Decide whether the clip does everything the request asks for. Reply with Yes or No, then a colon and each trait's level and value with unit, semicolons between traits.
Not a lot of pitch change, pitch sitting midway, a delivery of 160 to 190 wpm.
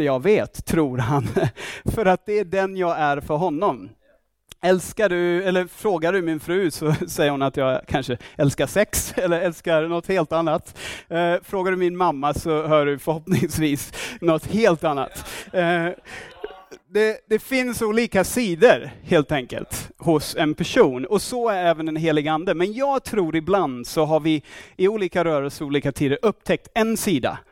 No: average, 4.0 semitones; medium, 170 Hz; average, 165 wpm